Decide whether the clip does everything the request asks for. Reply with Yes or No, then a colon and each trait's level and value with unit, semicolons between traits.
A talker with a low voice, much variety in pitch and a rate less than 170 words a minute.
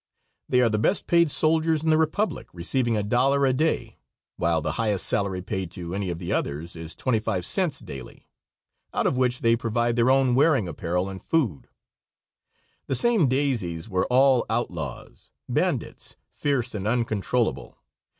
Yes: low, 115 Hz; wide, 6.8 semitones; average, 160 wpm